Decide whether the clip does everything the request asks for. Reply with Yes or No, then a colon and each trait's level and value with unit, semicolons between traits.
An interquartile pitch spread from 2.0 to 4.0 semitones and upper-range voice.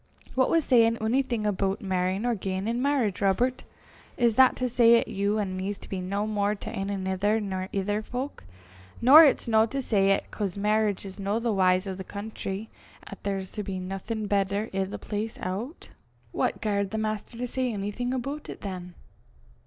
Yes: average, 3.1 semitones; high, 210 Hz